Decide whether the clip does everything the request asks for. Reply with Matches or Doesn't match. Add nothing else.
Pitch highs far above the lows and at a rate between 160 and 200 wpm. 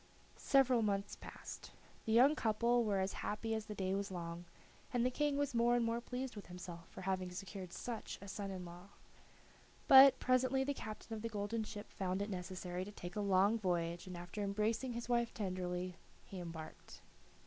Doesn't match